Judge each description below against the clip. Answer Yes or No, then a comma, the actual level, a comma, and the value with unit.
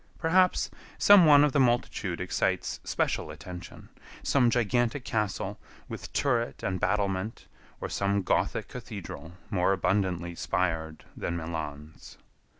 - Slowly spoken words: Yes, slow, 120 wpm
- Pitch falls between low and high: No, low, 100 Hz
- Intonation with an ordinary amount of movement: No, wide, 5.7 semitones